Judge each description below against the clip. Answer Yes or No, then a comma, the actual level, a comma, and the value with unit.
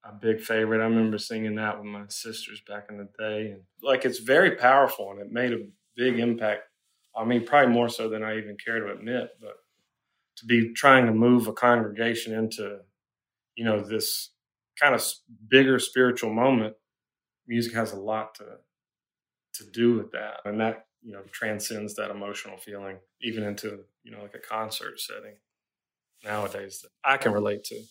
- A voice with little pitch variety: Yes, narrow, 1.9 semitones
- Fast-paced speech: No, average, 180 wpm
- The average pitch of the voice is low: Yes, low, 110 Hz